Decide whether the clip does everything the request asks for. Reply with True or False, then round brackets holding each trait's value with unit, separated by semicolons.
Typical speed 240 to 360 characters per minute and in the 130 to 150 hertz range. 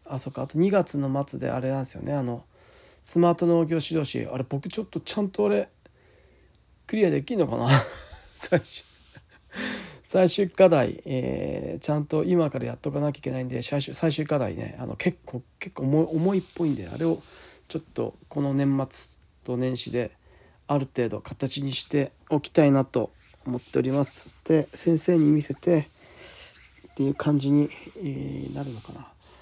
True (300 characters per minute; 140 Hz)